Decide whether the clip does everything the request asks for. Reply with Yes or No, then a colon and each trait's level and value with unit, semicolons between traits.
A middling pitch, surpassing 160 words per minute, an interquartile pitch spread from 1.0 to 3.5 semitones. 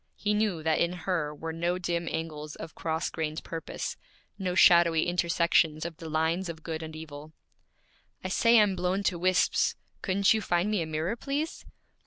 Yes: medium, 170 Hz; average, 180 wpm; average, 2.7 semitones